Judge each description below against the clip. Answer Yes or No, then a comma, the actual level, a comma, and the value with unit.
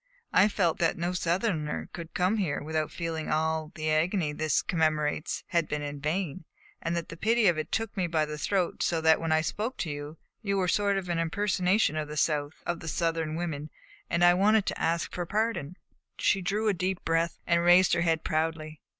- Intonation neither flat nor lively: Yes, average, 3.0 semitones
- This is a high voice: No, medium, 165 Hz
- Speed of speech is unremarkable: No, fast, 210 wpm